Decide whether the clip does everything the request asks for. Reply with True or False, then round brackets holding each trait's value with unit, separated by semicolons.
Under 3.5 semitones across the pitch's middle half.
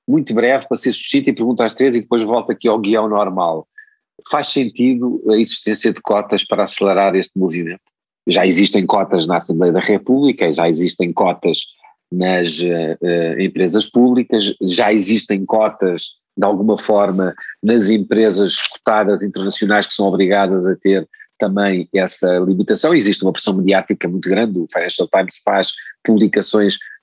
True (3.0 semitones)